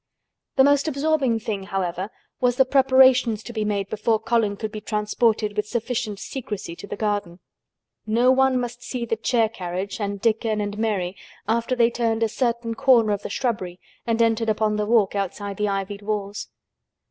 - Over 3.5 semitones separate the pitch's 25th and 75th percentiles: No, average, 2.7 semitones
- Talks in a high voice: Yes, high, 220 Hz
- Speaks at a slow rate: No, average, 180 wpm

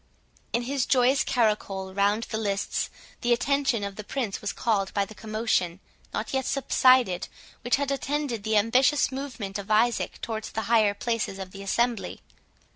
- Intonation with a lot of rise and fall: No, average, 4.0 semitones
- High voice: Yes, high, 225 Hz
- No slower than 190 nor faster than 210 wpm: No, average, 165 wpm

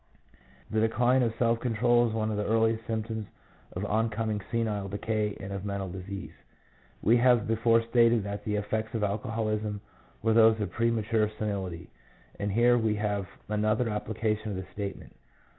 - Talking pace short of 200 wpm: Yes, average, 165 wpm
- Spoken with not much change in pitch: Yes, narrow, 1.7 semitones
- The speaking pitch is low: Yes, low, 110 Hz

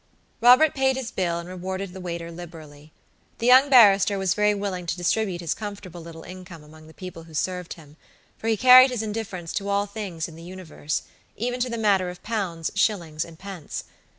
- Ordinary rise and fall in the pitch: Yes, average, 4.0 semitones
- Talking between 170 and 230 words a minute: Yes, average, 200 wpm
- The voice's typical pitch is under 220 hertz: Yes, medium, 185 Hz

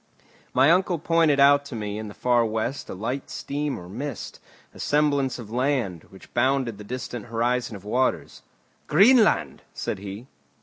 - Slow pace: No, average, 165 wpm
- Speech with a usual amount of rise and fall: Yes, average, 4.6 semitones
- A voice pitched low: Yes, low, 125 Hz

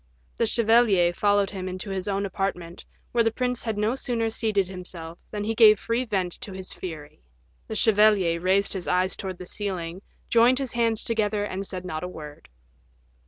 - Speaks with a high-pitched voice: Yes, high, 200 Hz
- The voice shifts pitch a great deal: No, average, 3.4 semitones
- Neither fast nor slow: Yes, average, 185 wpm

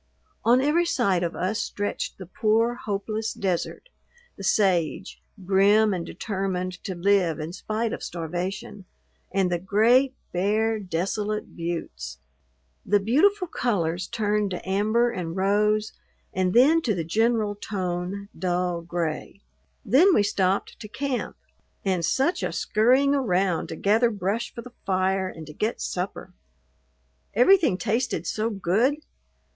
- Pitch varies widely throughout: No, average, 3.8 semitones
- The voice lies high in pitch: Yes, high, 200 Hz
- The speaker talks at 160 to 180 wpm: No, slow, 135 wpm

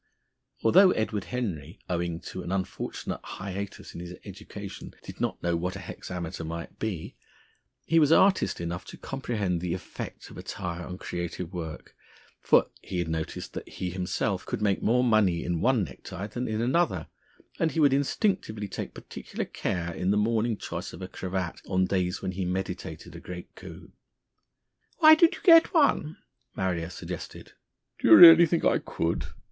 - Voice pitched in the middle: No, very low, 95 Hz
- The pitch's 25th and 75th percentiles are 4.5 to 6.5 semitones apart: Yes, average, 5.3 semitones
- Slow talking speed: No, average, 170 wpm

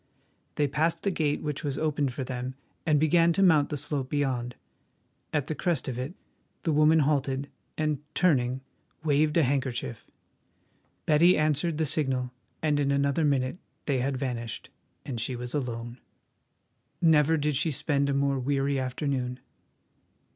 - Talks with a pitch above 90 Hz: Yes, medium, 140 Hz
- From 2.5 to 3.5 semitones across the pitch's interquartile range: Yes, average, 2.8 semitones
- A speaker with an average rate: Yes, average, 155 wpm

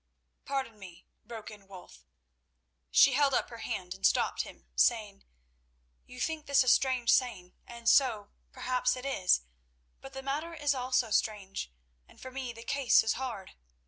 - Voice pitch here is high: Yes, high, 245 Hz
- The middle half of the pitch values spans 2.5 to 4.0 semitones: No, average, 4.8 semitones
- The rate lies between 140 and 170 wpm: Yes, average, 165 wpm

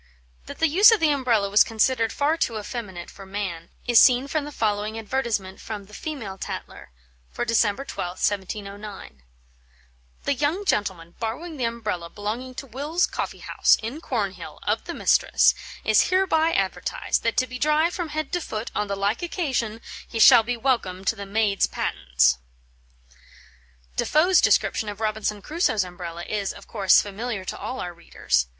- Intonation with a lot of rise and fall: Yes, wide, 5.7 semitones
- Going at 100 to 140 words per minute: No, average, 170 wpm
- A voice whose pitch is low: No, high, 220 Hz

